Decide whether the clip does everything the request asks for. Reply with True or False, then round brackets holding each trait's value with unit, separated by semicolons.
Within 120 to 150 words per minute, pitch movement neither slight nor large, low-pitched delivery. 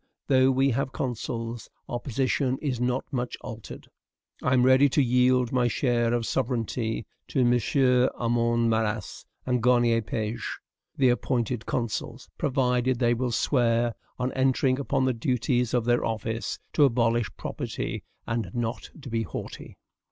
False (145 wpm; 1.9 semitones; 120 Hz)